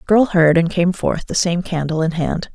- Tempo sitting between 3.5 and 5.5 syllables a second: Yes, 5.1 syllables/s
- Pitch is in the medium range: Yes, medium, 175 Hz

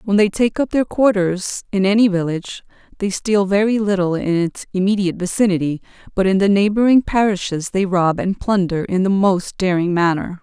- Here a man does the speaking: No, female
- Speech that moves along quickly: No, average, 180 wpm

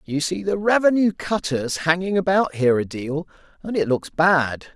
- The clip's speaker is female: No, male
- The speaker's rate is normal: Yes, average, 175 wpm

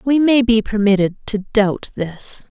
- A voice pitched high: Yes, high, 220 Hz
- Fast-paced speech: No, average, 160 wpm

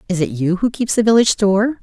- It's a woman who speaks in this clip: Yes, female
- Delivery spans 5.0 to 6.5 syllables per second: No, 6.7 syllables/s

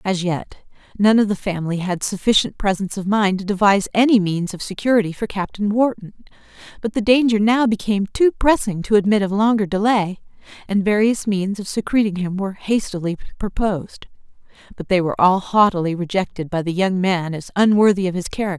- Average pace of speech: Yes, average, 180 wpm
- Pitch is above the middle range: Yes, high, 200 Hz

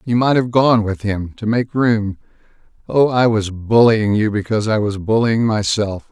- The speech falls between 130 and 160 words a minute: No, average, 185 wpm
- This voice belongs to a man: Yes, male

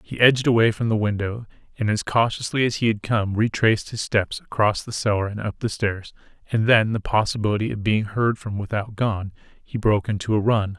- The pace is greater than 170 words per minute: Yes, fast, 205 wpm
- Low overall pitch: Yes, low, 110 Hz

